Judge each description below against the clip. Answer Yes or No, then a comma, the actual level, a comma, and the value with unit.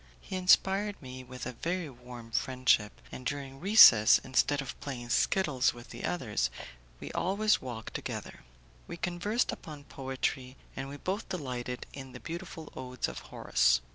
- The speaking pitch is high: No, low, 135 Hz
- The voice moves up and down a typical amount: No, wide, 5.8 semitones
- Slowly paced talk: No, average, 155 wpm